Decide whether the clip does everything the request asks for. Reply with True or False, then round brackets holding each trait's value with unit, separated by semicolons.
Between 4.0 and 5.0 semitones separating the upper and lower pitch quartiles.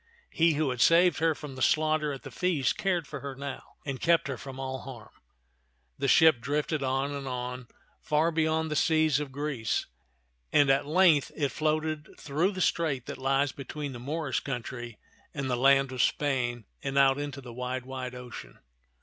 False (3.1 semitones)